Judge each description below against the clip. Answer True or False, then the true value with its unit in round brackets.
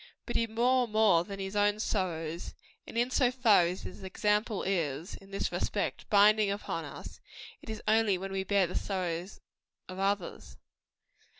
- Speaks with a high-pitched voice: True (200 Hz)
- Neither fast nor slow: True (170 wpm)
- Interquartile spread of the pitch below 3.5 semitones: True (2.7 semitones)